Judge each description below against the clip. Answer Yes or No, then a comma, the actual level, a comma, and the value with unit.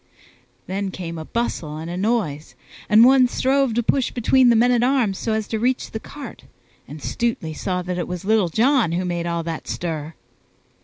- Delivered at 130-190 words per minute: No, average, 200 wpm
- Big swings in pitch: Yes, wide, 6.0 semitones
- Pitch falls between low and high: No, high, 205 Hz